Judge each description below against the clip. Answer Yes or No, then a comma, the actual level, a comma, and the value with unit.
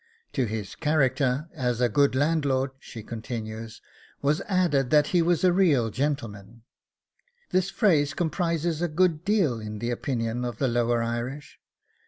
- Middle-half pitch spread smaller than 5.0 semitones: No, wide, 5.5 semitones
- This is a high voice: No, low, 135 Hz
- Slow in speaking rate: No, average, 150 wpm